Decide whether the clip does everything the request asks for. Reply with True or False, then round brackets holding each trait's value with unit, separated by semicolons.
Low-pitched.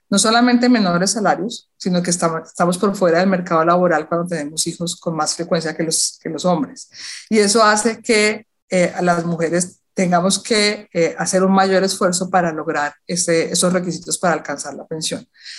False (180 Hz)